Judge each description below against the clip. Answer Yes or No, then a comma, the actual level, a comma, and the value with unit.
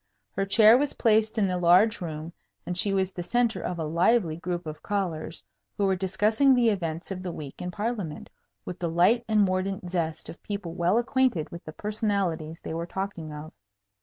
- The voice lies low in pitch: No, medium, 185 Hz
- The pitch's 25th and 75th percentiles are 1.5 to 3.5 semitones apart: No, average, 4.0 semitones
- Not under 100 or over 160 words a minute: No, average, 195 wpm